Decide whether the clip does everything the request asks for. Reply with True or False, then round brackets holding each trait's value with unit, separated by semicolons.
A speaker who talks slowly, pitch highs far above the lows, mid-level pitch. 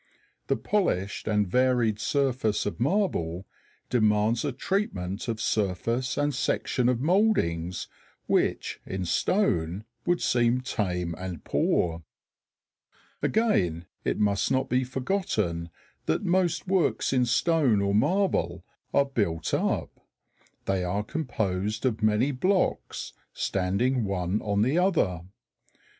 False (120 wpm; 6.5 semitones; 115 Hz)